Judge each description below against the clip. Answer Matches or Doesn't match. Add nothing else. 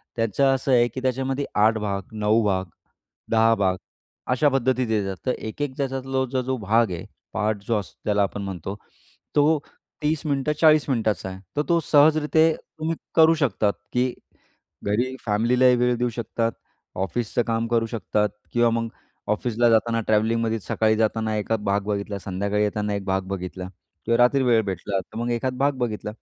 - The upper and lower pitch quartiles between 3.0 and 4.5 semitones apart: Matches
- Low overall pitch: Matches